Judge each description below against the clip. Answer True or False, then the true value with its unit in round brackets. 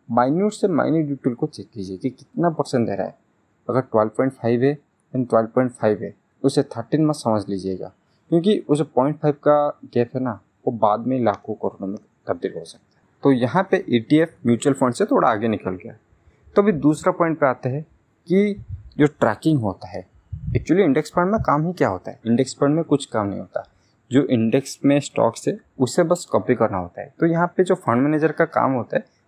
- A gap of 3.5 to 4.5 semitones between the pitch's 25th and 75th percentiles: False (5.2 semitones)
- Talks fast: True (225 wpm)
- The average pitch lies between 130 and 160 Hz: True (135 Hz)